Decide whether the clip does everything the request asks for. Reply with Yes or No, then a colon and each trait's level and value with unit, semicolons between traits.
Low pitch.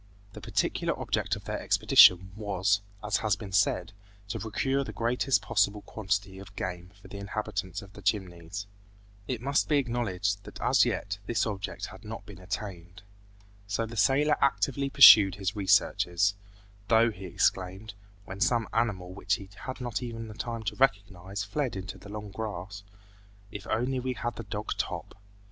Yes: low, 105 Hz